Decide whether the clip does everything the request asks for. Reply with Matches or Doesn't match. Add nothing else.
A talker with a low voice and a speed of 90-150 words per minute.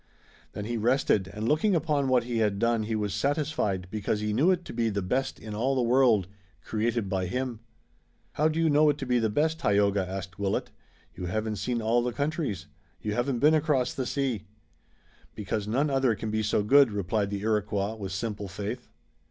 Doesn't match